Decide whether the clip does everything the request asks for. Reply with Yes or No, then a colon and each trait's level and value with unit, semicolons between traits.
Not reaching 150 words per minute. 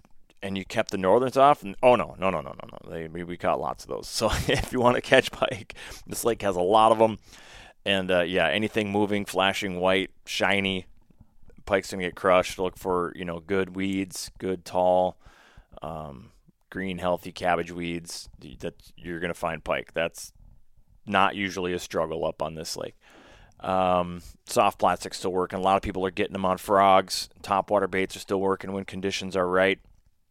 No: average, 190 wpm